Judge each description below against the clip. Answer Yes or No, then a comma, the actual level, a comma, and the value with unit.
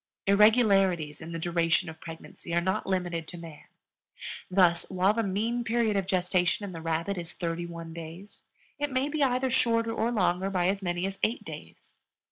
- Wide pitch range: No, average, 4.2 semitones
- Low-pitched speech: No, medium, 185 Hz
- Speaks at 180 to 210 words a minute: Yes, average, 185 wpm